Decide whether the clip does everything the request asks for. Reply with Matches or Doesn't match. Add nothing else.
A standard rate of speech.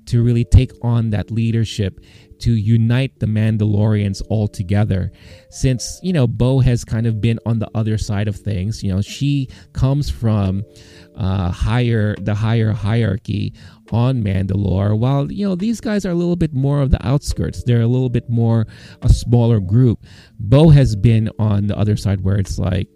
Matches